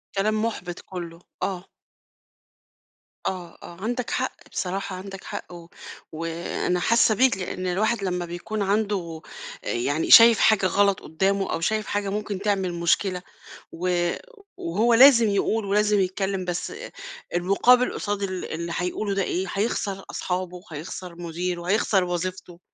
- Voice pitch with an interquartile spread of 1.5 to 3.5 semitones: Yes, average, 2.8 semitones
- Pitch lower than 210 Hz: Yes, high, 190 Hz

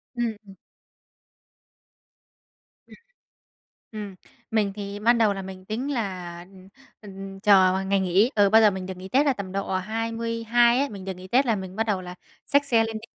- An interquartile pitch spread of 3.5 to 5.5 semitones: No, average, 3.1 semitones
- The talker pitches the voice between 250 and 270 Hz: No, high, 205 Hz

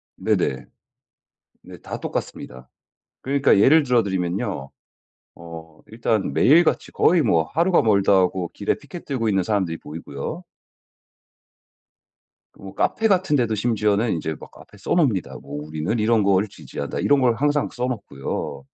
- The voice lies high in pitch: No, low, 105 Hz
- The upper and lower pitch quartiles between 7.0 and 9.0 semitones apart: Yes, wide, 7.5 semitones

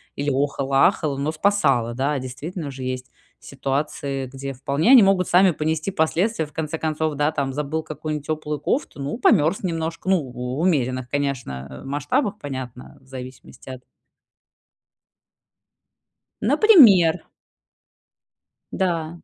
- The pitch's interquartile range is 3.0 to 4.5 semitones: Yes, average, 3.4 semitones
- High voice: No, medium, 150 Hz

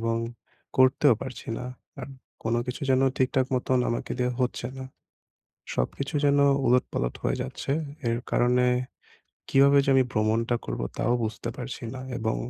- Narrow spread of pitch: Yes, narrow, 2.1 semitones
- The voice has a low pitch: Yes, low, 125 Hz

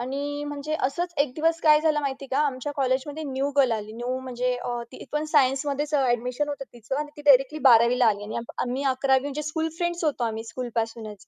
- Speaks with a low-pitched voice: No, very high, 270 Hz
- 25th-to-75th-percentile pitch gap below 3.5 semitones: Yes, average, 3.1 semitones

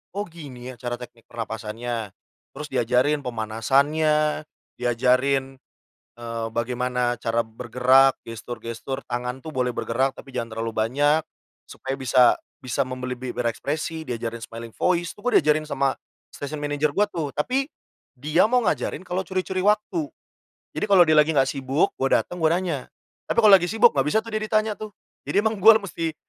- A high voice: No, low, 135 Hz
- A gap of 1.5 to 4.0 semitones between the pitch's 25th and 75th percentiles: No, average, 5.0 semitones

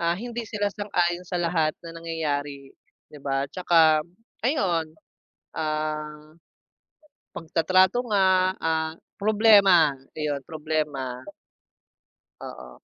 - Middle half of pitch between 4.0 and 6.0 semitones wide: No, average, 3.5 semitones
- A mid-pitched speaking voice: Yes, medium, 165 Hz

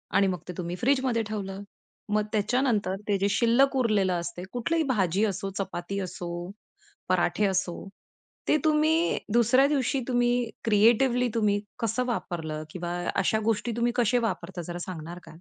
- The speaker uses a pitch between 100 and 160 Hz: No, high, 215 Hz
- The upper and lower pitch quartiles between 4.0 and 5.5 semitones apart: Yes, average, 4.7 semitones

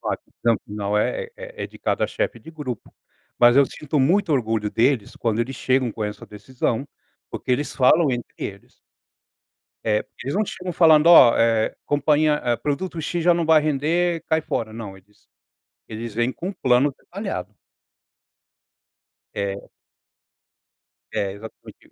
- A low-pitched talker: Yes, low, 130 Hz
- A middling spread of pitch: No, wide, 6.0 semitones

